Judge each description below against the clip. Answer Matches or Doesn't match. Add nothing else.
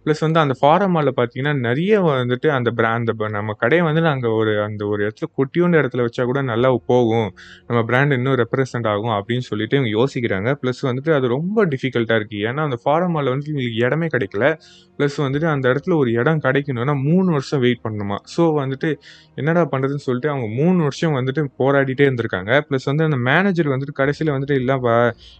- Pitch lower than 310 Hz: Matches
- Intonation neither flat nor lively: Matches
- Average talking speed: Doesn't match